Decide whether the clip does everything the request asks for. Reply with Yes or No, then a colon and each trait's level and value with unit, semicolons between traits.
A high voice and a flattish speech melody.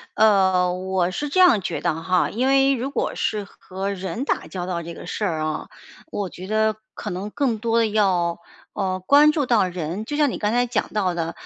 No: high, 200 Hz; average, 4.4 semitones